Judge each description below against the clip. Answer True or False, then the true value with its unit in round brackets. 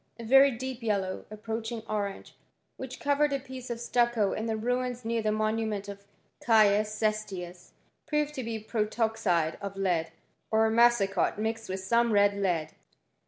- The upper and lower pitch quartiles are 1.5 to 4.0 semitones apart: True (2.9 semitones)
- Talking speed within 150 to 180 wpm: True (160 wpm)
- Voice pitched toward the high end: True (220 Hz)